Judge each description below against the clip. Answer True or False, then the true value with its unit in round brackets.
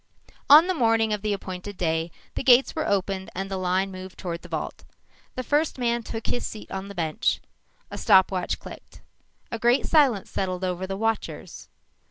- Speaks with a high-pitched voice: True (200 Hz)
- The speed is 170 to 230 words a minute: True (185 wpm)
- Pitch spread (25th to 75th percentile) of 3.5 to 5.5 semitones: True (4.1 semitones)